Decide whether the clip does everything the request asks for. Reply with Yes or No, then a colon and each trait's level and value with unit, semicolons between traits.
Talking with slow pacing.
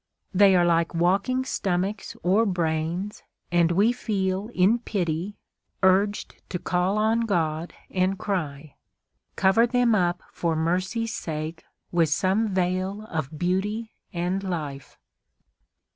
Yes: slow, 120 wpm